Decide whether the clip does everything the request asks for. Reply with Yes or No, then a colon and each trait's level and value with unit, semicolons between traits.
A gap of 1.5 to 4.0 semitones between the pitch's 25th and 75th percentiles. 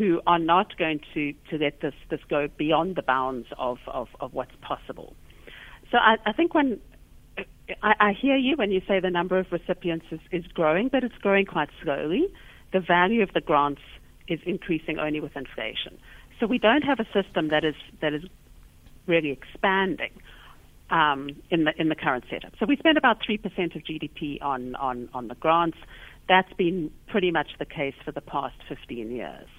No: average, 5.0 semitones